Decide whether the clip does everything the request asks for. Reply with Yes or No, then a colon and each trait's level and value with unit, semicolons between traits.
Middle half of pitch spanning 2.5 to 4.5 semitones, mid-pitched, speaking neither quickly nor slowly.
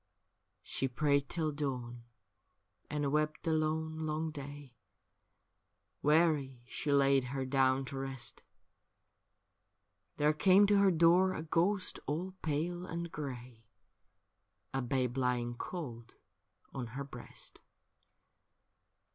No: average, 3.4 semitones; medium, 145 Hz; slow, 110 wpm